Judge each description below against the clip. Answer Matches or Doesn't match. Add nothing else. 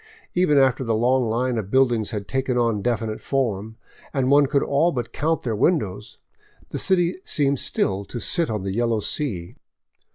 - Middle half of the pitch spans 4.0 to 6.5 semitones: Matches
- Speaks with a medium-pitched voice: Doesn't match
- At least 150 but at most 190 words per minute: Matches